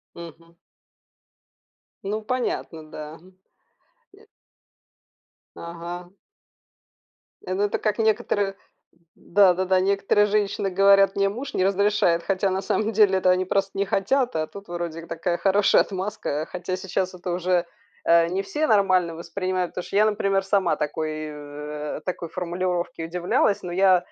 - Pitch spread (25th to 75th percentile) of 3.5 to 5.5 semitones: No, narrow, 2.5 semitones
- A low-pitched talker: No, medium, 185 Hz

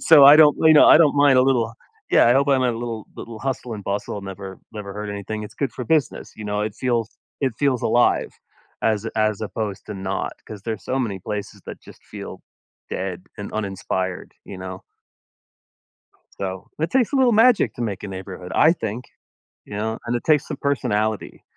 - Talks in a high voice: No, low, 110 Hz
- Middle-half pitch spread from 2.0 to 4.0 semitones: No, average, 4.8 semitones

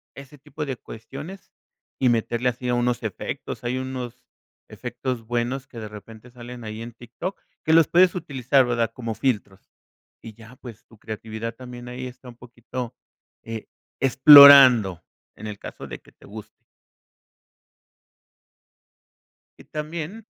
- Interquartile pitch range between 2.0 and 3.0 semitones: Yes, average, 2.7 semitones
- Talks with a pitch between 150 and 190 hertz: No, low, 125 Hz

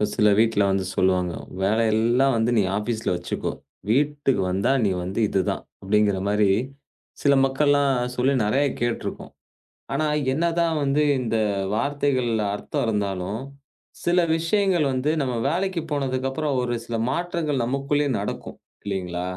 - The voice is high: No, low, 125 Hz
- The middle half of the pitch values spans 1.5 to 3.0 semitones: No, wide, 5.6 semitones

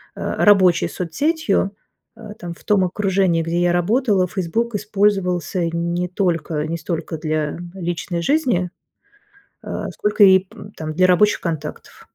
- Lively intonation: No, average, 3.3 semitones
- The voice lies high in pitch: No, medium, 180 Hz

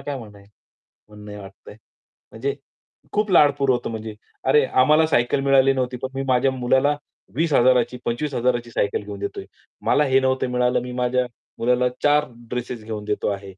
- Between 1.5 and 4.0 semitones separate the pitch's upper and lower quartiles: Yes, average, 3.2 semitones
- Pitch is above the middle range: No, low, 125 Hz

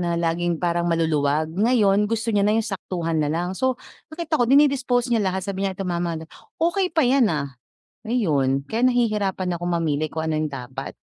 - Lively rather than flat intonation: Yes, wide, 6.4 semitones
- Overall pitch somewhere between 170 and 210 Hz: Yes, medium, 185 Hz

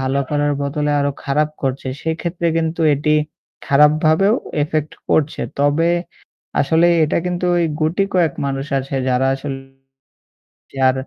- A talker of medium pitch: Yes, medium, 150 Hz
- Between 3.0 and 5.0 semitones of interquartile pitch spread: No, narrow, 2.6 semitones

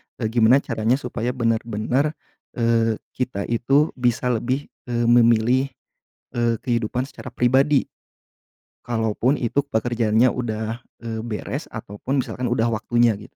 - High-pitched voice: No, low, 120 Hz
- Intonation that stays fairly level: Yes, narrow, 2.1 semitones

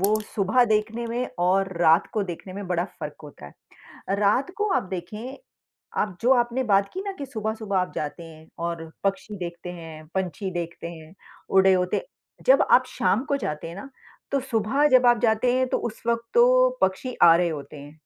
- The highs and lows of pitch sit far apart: Yes, wide, 5.9 semitones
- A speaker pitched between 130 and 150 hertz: No, high, 200 Hz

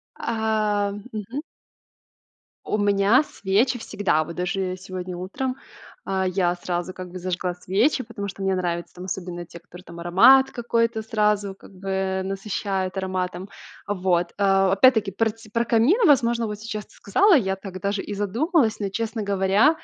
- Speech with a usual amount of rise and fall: Yes, average, 3.2 semitones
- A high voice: Yes, high, 195 Hz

